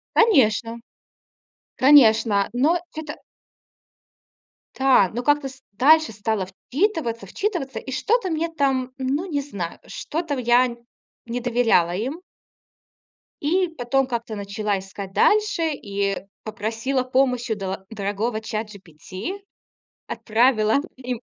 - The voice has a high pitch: Yes, high, 245 Hz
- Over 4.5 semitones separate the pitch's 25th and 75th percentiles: Yes, average, 5.1 semitones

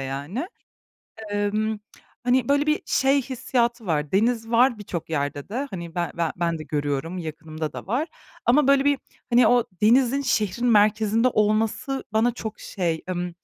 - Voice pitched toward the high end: Yes, high, 215 Hz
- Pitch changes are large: Yes, wide, 6.3 semitones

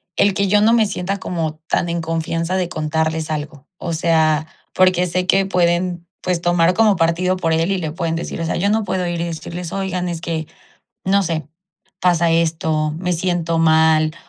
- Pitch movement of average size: No, narrow, 2.2 semitones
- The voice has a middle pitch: Yes, medium, 170 Hz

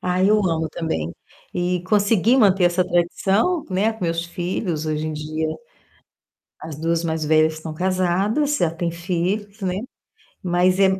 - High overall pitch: No, medium, 175 Hz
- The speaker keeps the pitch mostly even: No, average, 3.1 semitones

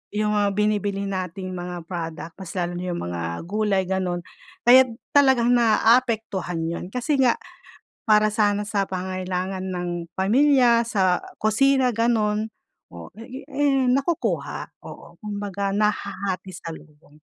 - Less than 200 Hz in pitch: No, high, 205 Hz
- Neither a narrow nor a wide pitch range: Yes, average, 4.1 semitones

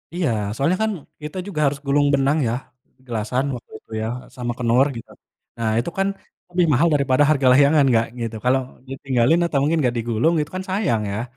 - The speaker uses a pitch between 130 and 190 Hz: Yes, low, 135 Hz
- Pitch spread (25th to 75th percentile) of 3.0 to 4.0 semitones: No, average, 4.5 semitones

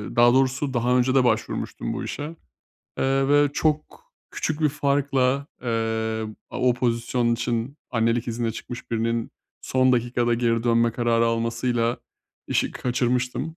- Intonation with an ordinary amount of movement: No, narrow, 2.2 semitones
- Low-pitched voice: Yes, low, 120 Hz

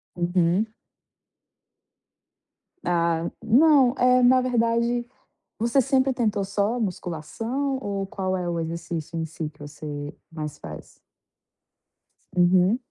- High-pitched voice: Yes, high, 195 Hz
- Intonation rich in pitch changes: Yes, wide, 6.3 semitones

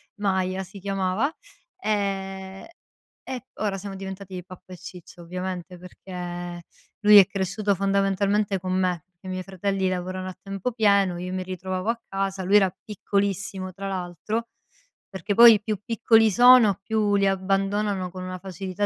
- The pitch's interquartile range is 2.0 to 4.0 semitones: No, narrow, 1.5 semitones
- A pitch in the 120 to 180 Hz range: No, high, 195 Hz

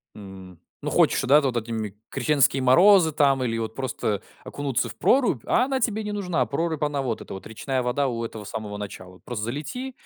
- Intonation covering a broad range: Yes, wide, 5.7 semitones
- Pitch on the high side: No, low, 130 Hz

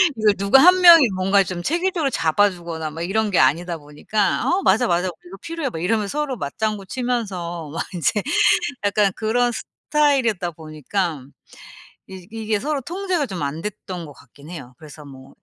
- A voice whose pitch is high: Yes, high, 195 Hz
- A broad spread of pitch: Yes, wide, 6.6 semitones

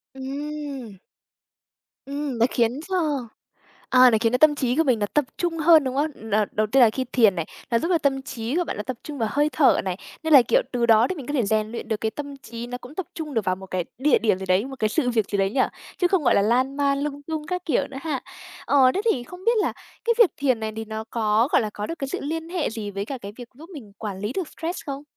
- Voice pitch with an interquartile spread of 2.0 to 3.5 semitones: No, average, 5.1 semitones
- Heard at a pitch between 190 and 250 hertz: No, very high, 260 Hz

